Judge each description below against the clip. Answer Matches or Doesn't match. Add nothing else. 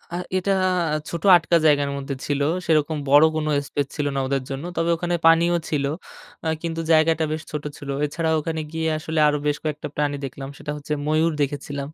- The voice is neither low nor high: Matches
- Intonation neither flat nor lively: Doesn't match